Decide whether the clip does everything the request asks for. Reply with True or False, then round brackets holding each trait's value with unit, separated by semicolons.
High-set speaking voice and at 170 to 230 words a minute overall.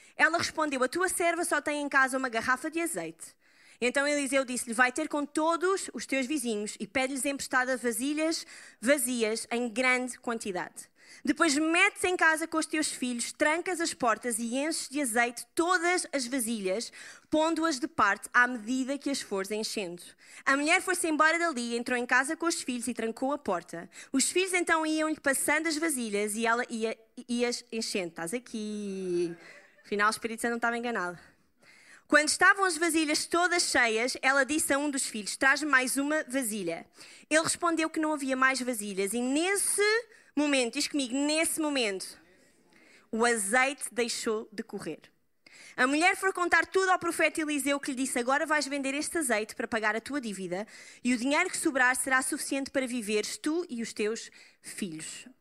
True (270 Hz; 175 wpm)